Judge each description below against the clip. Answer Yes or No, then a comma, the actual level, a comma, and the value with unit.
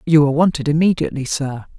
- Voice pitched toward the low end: No, medium, 150 Hz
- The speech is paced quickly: No, average, 170 wpm